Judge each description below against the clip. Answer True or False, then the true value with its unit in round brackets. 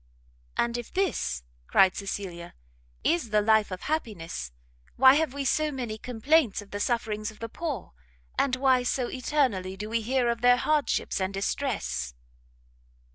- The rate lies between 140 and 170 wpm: True (155 wpm)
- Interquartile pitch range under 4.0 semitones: False (5.0 semitones)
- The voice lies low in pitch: False (235 Hz)